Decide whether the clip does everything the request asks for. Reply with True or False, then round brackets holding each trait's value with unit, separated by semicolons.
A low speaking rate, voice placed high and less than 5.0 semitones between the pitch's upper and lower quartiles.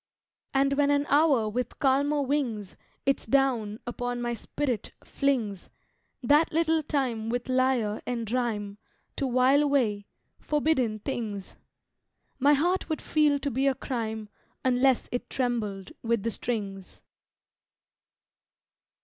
True (125 wpm; 250 Hz; 4.1 semitones)